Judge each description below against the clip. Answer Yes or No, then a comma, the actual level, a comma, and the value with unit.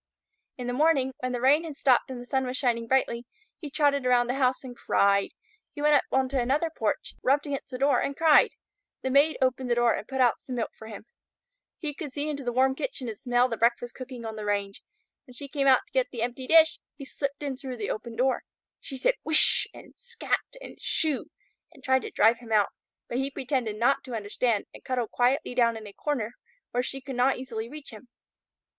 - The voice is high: Yes, very high, 255 Hz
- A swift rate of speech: Yes, fast, 230 wpm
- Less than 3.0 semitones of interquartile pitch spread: Yes, narrow, 2.6 semitones